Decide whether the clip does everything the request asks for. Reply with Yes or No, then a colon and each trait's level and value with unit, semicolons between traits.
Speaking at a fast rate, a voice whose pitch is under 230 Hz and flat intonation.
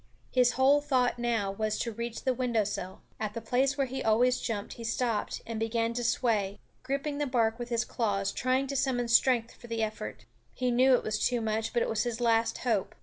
No: fast, 220 wpm; high, 235 Hz; narrow, 2.3 semitones